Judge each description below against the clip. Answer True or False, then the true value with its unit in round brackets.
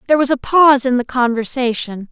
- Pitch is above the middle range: True (255 Hz)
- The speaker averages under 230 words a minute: True (200 wpm)